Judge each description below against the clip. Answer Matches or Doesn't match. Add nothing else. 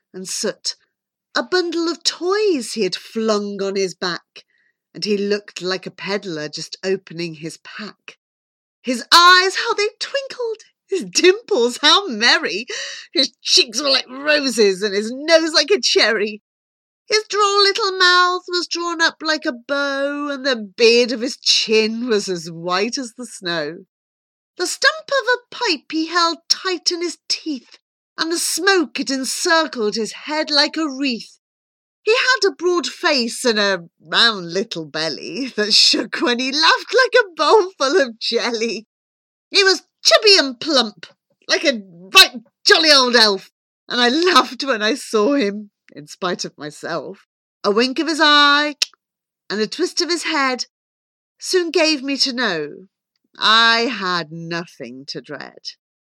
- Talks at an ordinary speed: Matches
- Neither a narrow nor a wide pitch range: Doesn't match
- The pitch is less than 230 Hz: Doesn't match